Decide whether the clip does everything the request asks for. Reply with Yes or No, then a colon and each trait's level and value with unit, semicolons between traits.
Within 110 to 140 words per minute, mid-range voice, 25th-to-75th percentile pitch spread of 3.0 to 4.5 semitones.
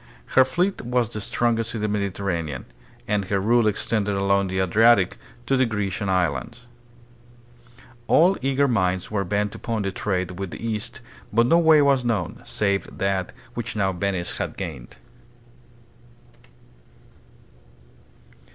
No: slow, 135 wpm; low, 105 Hz; average, 3.8 semitones